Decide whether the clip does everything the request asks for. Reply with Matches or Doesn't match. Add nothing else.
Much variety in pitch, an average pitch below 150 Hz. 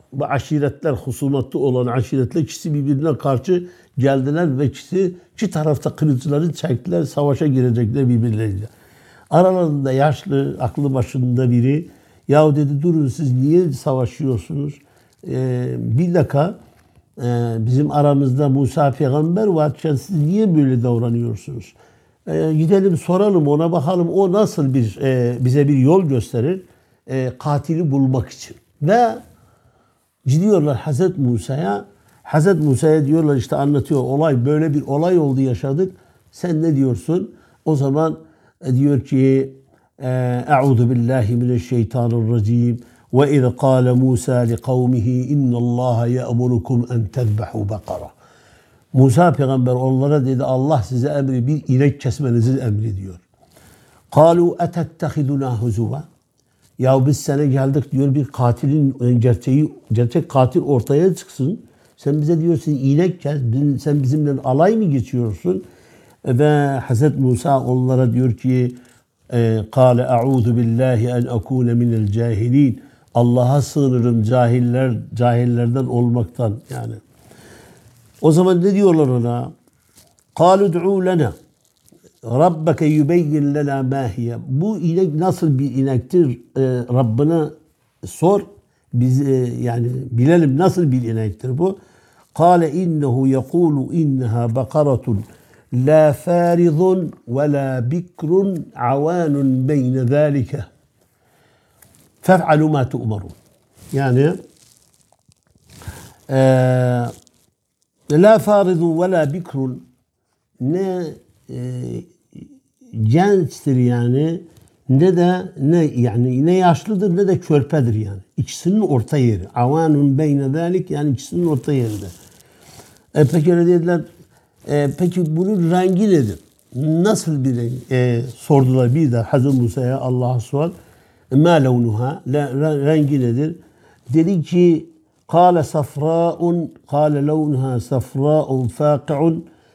Doesn't match